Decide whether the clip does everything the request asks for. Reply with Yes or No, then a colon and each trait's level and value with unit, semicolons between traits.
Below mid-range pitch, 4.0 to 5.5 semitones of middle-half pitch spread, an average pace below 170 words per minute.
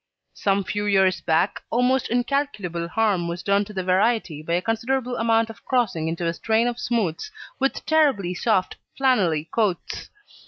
No: high, 205 Hz; average, 5.1 semitones; average, 160 wpm